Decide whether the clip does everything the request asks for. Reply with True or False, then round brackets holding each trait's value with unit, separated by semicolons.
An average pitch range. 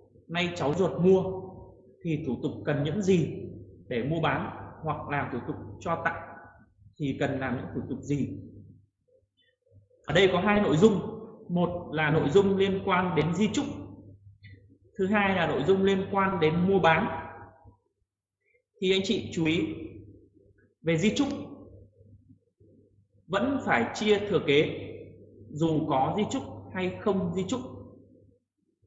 False (7.4 semitones)